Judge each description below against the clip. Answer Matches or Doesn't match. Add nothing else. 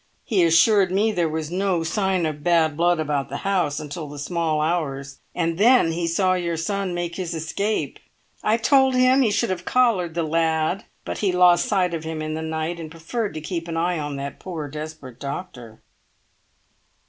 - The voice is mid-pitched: Matches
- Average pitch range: Matches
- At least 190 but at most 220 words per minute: Matches